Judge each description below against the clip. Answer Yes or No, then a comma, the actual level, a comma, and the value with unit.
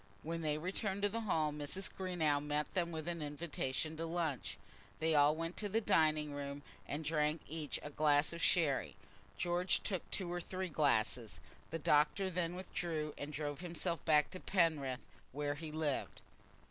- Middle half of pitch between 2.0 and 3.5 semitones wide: Yes, average, 3.0 semitones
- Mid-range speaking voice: Yes, medium, 155 Hz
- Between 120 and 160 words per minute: No, average, 170 wpm